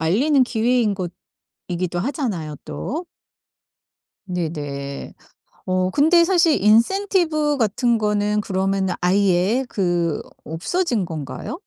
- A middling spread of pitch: No, wide, 7.4 semitones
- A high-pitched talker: Yes, high, 205 Hz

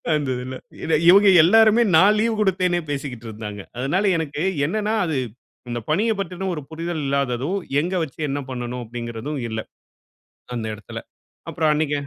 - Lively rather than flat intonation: Yes, wide, 6.9 semitones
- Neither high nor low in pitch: Yes, medium, 150 Hz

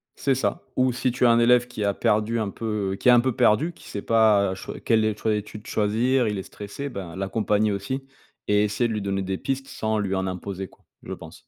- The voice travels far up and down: No, average, 3.2 semitones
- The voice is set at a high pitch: No, low, 105 Hz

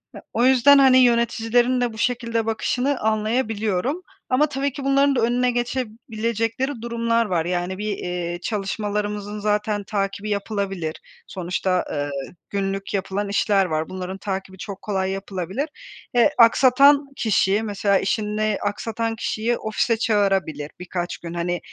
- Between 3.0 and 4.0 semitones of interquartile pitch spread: Yes, average, 3.5 semitones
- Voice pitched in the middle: No, high, 215 Hz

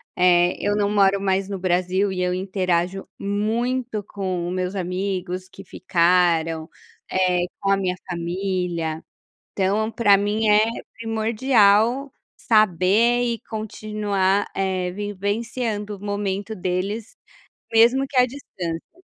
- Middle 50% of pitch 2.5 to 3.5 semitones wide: Yes, average, 2.9 semitones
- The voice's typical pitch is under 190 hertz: No, high, 195 Hz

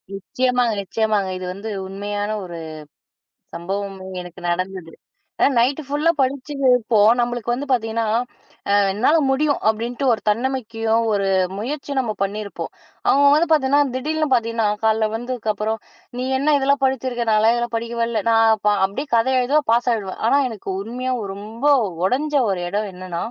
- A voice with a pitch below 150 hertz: No, high, 230 Hz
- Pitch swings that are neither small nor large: Yes, average, 4.0 semitones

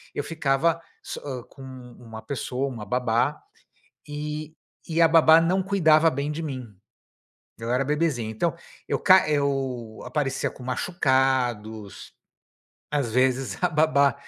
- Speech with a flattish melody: No, average, 3.8 semitones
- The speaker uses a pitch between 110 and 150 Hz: Yes, medium, 140 Hz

